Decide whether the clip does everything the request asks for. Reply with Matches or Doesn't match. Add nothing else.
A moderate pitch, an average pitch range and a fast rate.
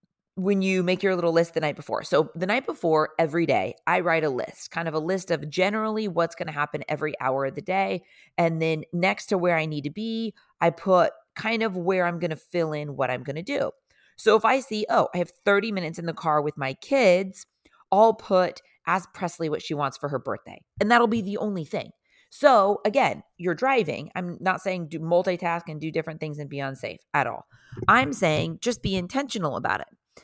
Matches